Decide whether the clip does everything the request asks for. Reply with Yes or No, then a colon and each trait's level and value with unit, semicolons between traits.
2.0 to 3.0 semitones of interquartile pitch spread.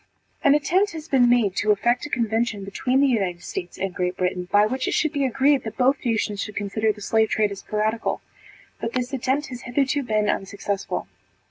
No: average, 4.3 semitones